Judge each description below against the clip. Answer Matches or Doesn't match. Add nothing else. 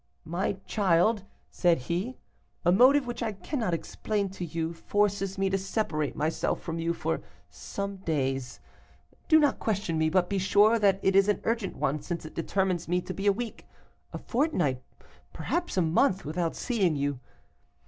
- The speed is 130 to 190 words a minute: Matches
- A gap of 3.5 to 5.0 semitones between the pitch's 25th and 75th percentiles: Matches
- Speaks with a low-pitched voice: Doesn't match